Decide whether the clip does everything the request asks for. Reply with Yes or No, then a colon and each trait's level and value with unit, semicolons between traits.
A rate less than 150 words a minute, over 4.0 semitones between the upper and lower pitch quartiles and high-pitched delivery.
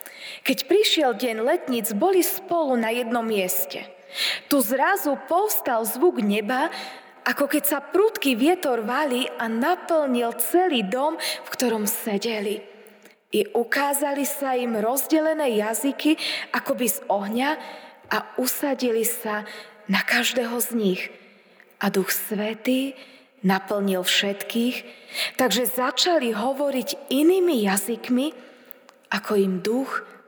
Yes: average, 115 wpm; average, 4.4 semitones; very high, 250 Hz